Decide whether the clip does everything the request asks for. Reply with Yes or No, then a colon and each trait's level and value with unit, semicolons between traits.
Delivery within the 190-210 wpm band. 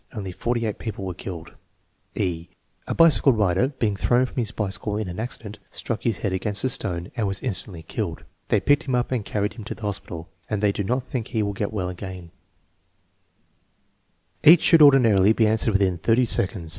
Yes: fast, 205 wpm